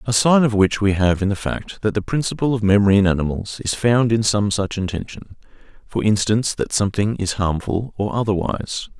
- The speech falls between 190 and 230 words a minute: Yes, average, 200 wpm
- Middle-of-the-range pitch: No, low, 105 Hz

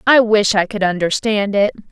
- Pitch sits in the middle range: No, high, 205 Hz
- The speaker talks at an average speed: Yes, average, 190 wpm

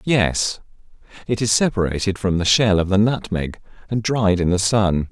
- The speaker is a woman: No, male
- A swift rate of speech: No, average, 175 wpm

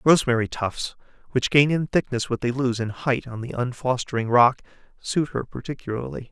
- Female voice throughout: No, male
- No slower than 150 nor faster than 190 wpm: Yes, average, 170 wpm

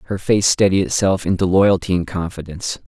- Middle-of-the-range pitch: No, very low, 95 Hz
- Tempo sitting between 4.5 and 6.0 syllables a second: Yes, 5.7 syllables/s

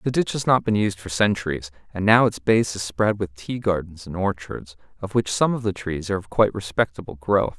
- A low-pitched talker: Yes, low, 100 Hz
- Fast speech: Yes, fast, 235 wpm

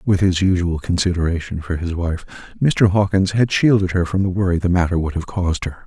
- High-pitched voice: No, very low, 90 Hz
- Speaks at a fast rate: Yes, fast, 215 wpm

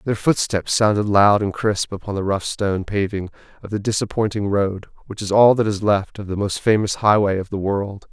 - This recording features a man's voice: Yes, male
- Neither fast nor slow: No, fast, 215 wpm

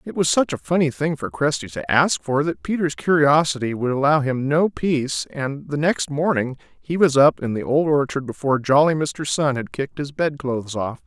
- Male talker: Yes, male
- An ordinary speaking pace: No, fast, 210 wpm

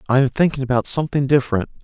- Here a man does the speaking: Yes, male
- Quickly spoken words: No, average, 195 wpm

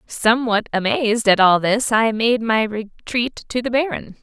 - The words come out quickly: No, average, 170 wpm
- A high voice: Yes, high, 225 Hz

